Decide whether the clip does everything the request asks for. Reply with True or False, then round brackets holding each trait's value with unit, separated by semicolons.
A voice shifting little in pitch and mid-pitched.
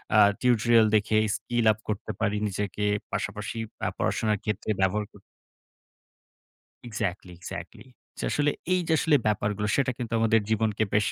False (1.8 semitones; 110 Hz)